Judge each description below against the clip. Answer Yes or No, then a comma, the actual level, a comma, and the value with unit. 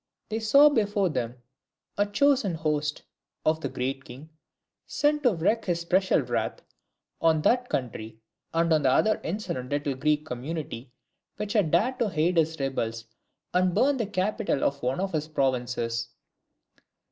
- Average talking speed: Yes, average, 155 wpm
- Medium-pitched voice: Yes, medium, 160 Hz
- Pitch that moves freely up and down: Yes, wide, 7.3 semitones